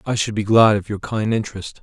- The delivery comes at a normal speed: No, fast, 265 wpm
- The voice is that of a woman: No, male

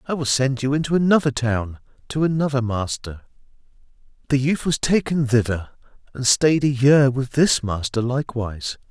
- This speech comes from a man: Yes, male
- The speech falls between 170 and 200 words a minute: No, average, 155 wpm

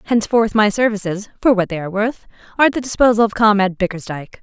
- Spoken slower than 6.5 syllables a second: No, 7.3 syllables/s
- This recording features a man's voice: No, female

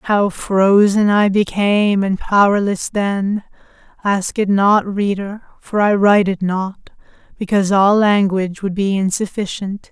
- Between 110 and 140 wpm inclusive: Yes, slow, 135 wpm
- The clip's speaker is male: No, female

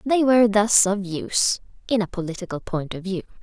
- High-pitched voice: Yes, high, 200 Hz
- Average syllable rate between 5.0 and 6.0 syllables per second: Yes, 5.5 syllables/s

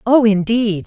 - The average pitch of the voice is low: No, high, 220 Hz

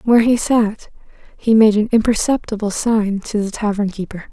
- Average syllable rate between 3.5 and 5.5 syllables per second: Yes, 5.3 syllables/s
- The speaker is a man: No, female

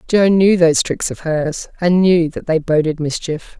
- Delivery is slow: No, average, 200 wpm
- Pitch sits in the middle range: Yes, medium, 165 Hz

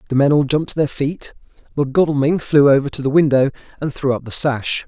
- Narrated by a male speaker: Yes, male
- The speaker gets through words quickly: Yes, fast, 235 wpm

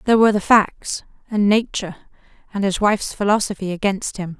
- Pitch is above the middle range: Yes, high, 200 Hz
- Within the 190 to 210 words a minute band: No, average, 165 wpm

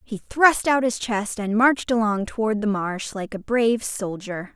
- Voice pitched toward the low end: No, high, 220 Hz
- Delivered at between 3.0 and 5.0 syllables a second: Yes, 4.6 syllables/s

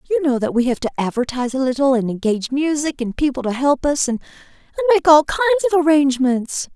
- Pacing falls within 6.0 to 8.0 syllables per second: Yes, 6.4 syllables/s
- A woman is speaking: Yes, female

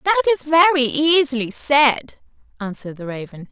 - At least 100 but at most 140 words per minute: Yes, slow, 135 wpm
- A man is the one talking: No, female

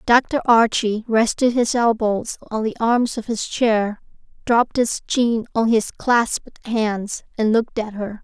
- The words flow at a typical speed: Yes, average, 160 wpm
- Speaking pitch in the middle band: No, high, 225 Hz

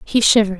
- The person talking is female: Yes, female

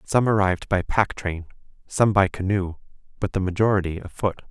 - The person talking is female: No, male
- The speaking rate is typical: Yes, average, 160 wpm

